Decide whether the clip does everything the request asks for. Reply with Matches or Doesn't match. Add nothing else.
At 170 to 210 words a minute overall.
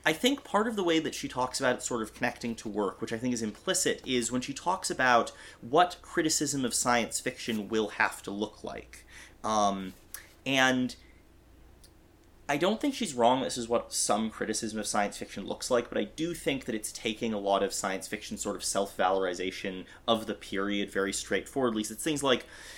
Matches